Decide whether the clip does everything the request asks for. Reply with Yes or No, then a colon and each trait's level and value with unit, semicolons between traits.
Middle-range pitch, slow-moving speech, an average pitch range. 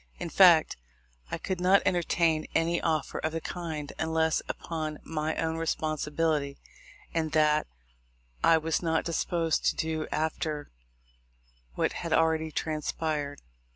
No: medium, 160 Hz; slow, 130 wpm; narrow, 1.0 semitones